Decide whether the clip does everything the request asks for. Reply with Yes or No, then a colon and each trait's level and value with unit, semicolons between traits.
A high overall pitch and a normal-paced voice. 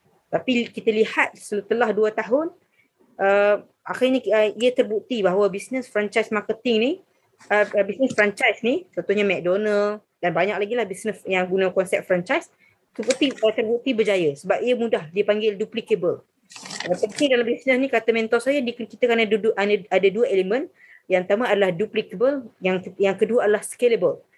No: high, 220 Hz; fast, 160 wpm